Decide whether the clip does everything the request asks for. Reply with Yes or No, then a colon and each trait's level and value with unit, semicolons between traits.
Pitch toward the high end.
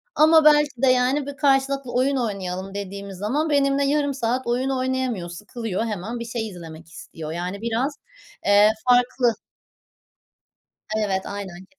Yes: high, 240 Hz